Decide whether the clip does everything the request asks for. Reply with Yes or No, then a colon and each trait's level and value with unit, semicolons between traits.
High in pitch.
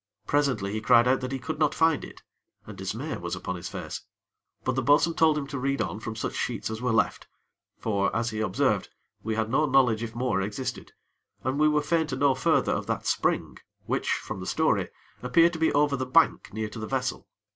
No: low, 130 Hz